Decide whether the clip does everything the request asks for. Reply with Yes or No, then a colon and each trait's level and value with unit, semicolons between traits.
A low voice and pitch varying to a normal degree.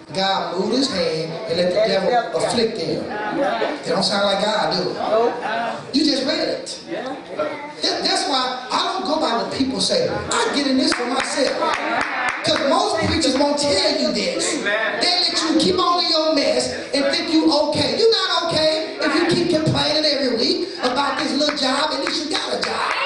No: very high, 295 Hz; average, 4.6 semitones